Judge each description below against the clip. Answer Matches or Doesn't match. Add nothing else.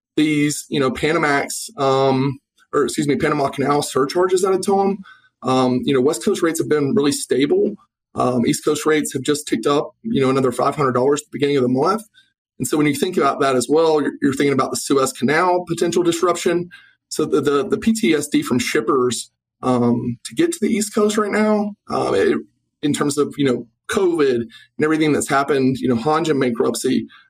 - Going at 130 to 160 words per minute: Doesn't match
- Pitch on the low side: Doesn't match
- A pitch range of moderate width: Doesn't match